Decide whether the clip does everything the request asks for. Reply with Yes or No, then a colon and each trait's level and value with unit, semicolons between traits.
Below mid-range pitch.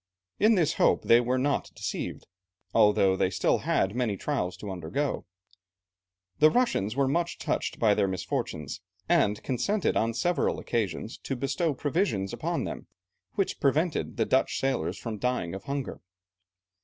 Yes: low, 125 Hz